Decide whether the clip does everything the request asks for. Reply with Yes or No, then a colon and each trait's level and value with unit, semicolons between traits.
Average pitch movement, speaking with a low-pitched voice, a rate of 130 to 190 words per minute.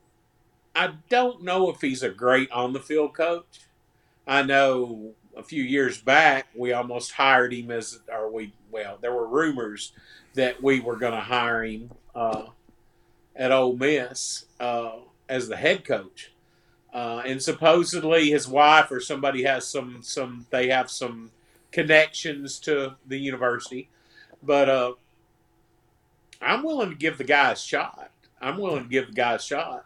Yes: average, 3.0 semitones; low, 130 Hz; average, 160 wpm